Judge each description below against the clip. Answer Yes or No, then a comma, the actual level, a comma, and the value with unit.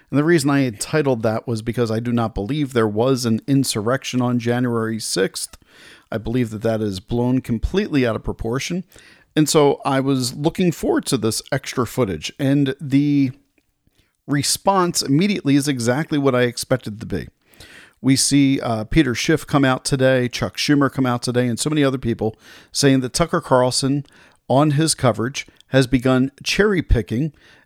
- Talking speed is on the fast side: No, average, 175 wpm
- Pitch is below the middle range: Yes, low, 130 Hz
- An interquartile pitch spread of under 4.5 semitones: Yes, average, 3.3 semitones